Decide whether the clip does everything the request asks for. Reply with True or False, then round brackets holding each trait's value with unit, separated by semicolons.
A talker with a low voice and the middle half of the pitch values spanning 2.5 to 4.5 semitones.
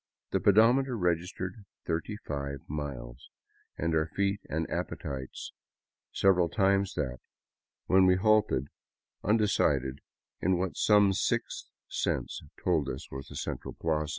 False (85 Hz; 5.5 semitones)